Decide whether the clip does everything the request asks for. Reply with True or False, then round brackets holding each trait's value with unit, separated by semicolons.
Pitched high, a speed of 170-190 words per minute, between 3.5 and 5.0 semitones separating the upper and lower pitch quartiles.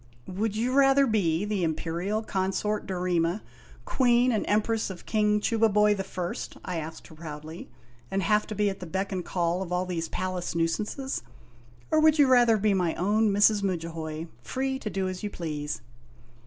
True (195 Hz; 180 wpm; 3.9 semitones)